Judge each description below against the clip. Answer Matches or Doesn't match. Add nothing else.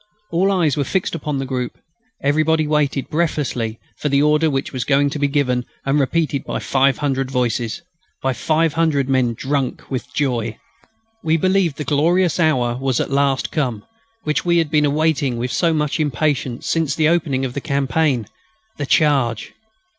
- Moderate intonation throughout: Matches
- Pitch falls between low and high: Matches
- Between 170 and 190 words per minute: Matches